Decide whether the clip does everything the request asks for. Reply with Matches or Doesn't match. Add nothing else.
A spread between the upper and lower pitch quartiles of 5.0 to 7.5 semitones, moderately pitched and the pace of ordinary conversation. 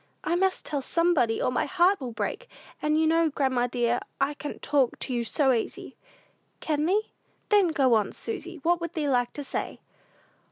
Doesn't match